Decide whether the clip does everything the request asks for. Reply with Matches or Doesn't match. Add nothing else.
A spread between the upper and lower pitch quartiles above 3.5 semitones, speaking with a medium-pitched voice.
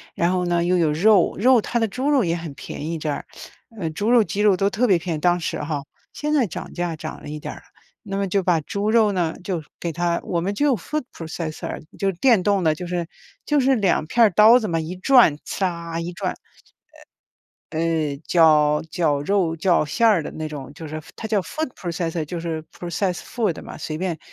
Matches